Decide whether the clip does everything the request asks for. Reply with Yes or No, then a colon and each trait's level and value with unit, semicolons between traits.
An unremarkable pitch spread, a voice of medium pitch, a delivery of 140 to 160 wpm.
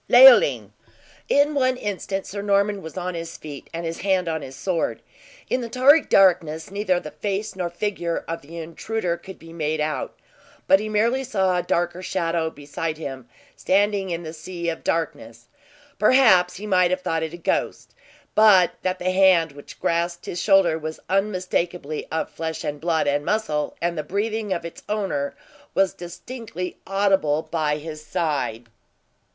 No: average, 3.6 semitones; medium, 175 Hz; average, 170 wpm